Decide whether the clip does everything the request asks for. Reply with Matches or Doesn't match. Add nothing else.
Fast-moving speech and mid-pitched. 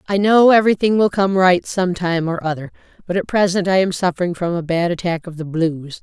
Matches